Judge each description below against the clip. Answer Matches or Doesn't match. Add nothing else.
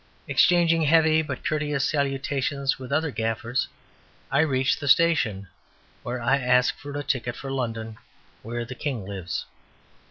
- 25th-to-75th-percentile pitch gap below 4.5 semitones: Matches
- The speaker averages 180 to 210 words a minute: Doesn't match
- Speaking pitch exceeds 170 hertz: Doesn't match